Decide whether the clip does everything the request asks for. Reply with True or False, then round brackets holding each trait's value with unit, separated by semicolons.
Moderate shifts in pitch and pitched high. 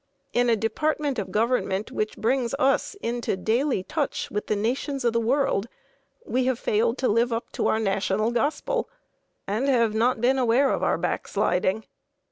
True (3.3 semitones; 235 Hz)